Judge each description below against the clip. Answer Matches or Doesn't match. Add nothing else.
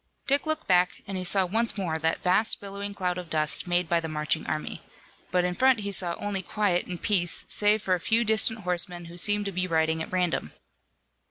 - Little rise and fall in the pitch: Doesn't match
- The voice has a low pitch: Doesn't match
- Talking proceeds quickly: Matches